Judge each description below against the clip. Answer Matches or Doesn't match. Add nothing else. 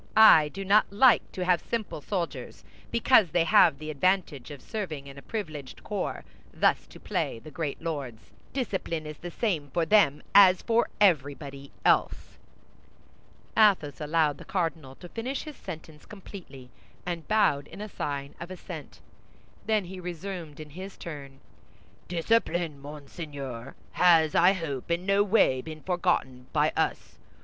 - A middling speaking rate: Matches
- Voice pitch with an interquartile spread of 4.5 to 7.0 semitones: Matches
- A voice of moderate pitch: Matches